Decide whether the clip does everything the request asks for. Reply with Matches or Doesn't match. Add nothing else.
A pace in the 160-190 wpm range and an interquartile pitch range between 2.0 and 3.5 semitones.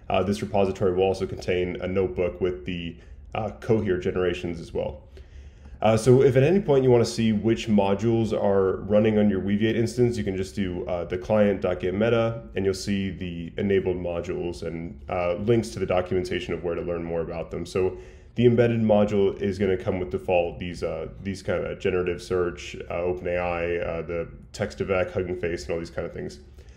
Doesn't match